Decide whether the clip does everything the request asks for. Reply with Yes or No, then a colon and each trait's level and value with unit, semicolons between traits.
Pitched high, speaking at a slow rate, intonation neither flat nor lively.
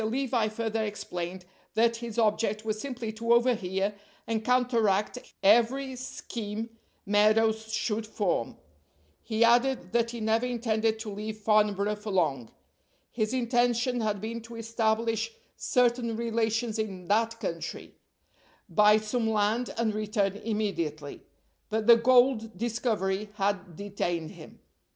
No: high, 220 Hz; slow, 125 wpm; narrow, 2.0 semitones